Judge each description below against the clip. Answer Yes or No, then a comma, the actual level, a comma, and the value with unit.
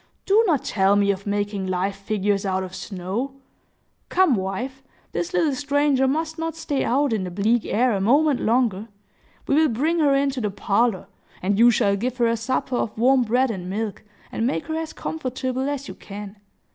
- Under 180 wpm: No, average, 195 wpm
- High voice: Yes, high, 235 Hz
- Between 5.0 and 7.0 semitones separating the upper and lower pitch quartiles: Yes, wide, 5.5 semitones